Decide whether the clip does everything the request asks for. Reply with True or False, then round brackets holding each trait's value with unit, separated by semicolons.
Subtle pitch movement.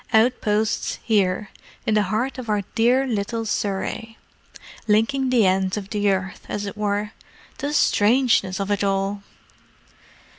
True (2.2 semitones)